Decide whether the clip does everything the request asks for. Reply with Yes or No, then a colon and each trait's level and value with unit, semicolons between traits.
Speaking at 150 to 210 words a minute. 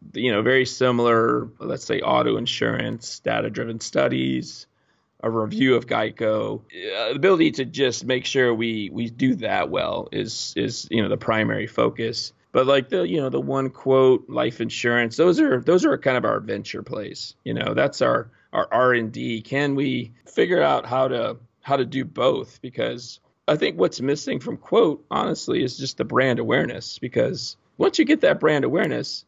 Yes: average, 185 wpm